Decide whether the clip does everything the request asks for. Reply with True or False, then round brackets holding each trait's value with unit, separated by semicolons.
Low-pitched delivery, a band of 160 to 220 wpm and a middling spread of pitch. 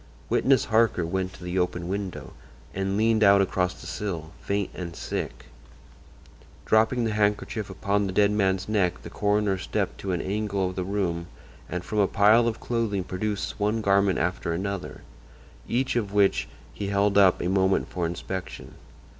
False (100 Hz; 170 wpm; 2.1 semitones)